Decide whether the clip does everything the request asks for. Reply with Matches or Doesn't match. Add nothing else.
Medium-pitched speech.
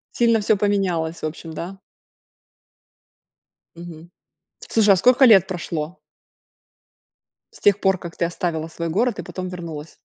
Matches